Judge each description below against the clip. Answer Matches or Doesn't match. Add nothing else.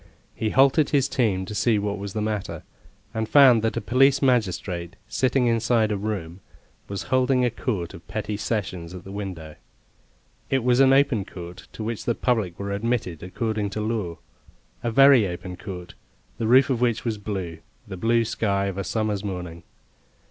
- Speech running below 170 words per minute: Doesn't match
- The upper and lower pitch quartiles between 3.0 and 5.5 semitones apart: Matches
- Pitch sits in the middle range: Doesn't match